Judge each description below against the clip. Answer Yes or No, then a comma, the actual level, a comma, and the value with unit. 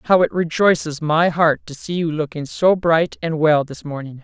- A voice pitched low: No, medium, 160 Hz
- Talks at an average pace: No, fast, 215 wpm